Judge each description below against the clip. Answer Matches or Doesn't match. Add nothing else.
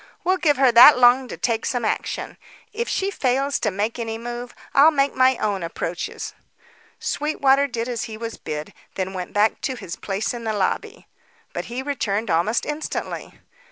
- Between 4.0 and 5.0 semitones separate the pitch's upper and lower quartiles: Matches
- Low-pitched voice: Doesn't match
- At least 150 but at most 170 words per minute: Doesn't match